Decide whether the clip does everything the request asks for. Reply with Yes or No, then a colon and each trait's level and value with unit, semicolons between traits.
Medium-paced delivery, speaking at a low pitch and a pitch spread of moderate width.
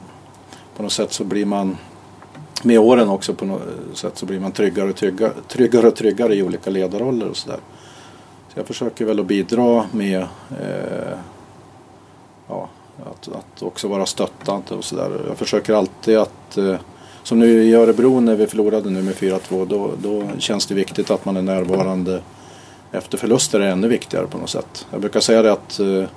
Yes: average, 185 wpm; low, 105 Hz; average, 3.3 semitones